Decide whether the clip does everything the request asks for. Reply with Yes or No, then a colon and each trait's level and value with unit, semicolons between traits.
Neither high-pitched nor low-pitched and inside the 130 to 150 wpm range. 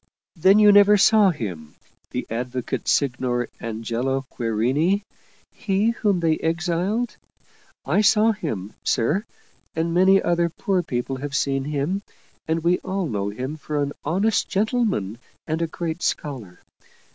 Yes: medium, 160 Hz; average, 140 wpm